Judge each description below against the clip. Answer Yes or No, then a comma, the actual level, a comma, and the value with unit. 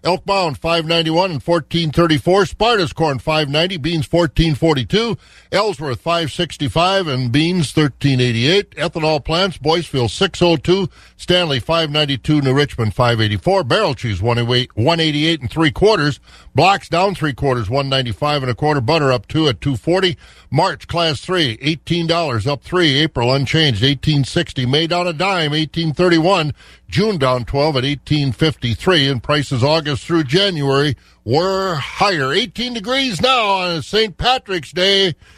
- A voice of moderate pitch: Yes, medium, 160 Hz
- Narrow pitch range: No, average, 4.3 semitones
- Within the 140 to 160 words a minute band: Yes, average, 155 wpm